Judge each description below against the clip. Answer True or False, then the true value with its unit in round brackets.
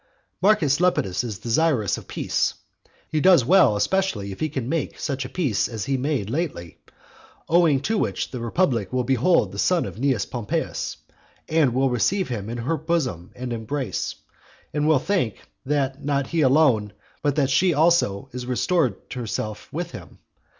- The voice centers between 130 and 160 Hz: True (135 Hz)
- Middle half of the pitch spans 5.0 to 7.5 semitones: True (5.5 semitones)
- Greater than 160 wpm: True (170 wpm)